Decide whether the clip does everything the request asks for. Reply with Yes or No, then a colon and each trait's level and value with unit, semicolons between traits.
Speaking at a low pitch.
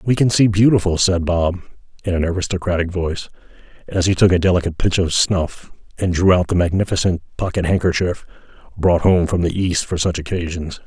Yes: very low, 90 Hz